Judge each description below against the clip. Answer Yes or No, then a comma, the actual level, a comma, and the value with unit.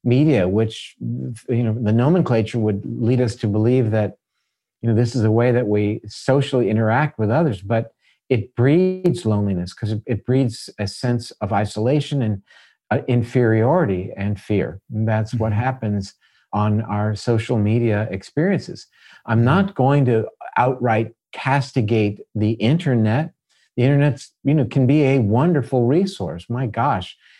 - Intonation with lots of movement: No, average, 3.5 semitones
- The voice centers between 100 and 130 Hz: Yes, low, 115 Hz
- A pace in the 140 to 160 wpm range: Yes, average, 150 wpm